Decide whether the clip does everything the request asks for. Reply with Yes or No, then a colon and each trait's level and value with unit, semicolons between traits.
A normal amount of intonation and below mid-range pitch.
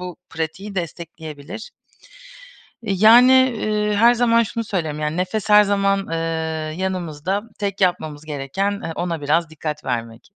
No: average, 4.9 semitones; medium, 185 Hz